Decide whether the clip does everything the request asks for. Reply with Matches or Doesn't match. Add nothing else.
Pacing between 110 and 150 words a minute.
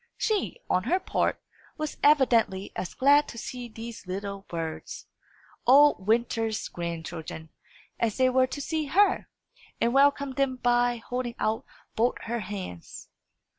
Matches